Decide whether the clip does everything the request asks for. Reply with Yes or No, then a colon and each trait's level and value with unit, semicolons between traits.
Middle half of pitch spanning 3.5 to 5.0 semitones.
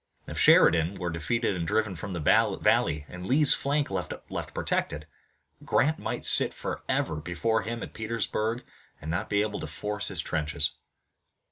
No: wide, 5.6 semitones